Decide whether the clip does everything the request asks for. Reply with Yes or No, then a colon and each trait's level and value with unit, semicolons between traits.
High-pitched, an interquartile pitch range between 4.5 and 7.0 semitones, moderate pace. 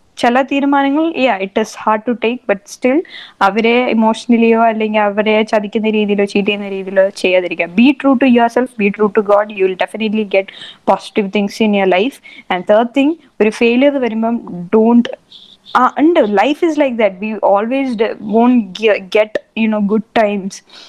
No: high, 220 Hz; average, 3.4 semitones; average, 160 wpm